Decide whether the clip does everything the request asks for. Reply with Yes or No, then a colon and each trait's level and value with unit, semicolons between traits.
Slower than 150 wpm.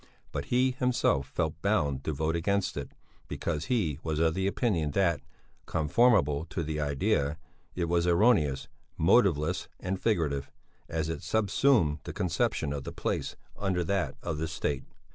No: average, 155 wpm